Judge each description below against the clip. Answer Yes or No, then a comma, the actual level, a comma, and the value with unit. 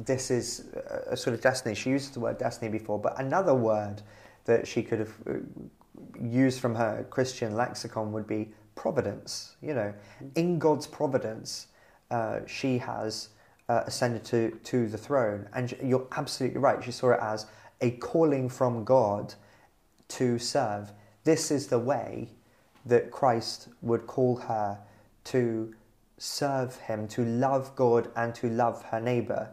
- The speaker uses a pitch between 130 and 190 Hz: No, low, 120 Hz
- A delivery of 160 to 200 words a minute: No, average, 150 wpm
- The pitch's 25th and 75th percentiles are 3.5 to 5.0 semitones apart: No, average, 2.9 semitones